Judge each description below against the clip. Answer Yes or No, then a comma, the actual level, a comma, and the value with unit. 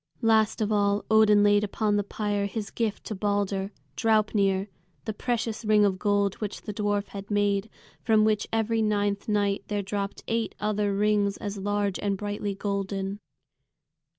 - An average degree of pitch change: No, narrow, 1.0 semitones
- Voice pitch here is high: Yes, high, 205 Hz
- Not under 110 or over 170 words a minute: Yes, average, 160 wpm